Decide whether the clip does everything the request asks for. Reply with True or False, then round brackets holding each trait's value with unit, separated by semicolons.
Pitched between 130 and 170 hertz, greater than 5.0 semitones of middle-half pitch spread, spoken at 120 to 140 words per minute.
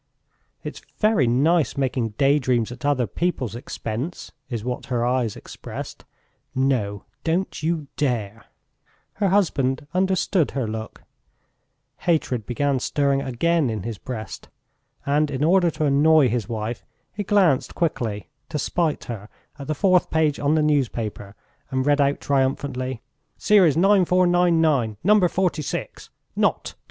True (140 Hz; 5.4 semitones; 135 wpm)